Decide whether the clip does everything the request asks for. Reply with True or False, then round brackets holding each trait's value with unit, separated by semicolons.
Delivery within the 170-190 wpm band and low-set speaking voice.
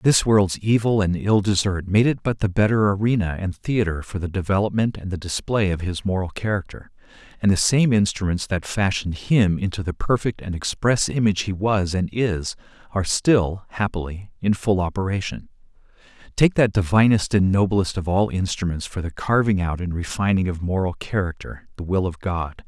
True (180 wpm; 95 Hz)